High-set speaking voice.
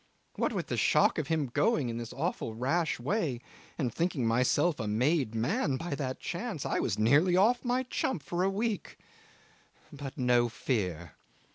No: medium, 145 Hz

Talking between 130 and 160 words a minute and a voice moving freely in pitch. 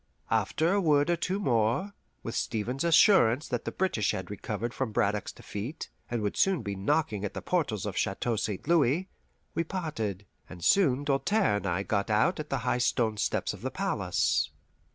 No: average, 190 wpm; wide, 7.6 semitones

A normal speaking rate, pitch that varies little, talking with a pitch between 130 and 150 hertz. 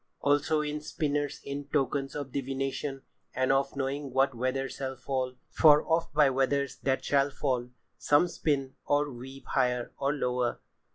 Yes: average, 150 wpm; narrow, 1.6 semitones; low, 135 Hz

